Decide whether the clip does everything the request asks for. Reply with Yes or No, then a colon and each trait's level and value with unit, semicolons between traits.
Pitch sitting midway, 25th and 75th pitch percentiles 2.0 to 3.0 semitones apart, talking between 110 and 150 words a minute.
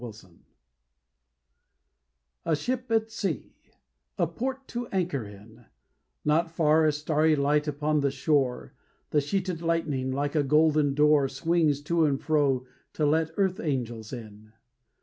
No: medium, 150 Hz; average, 3.5 semitones; average, 140 wpm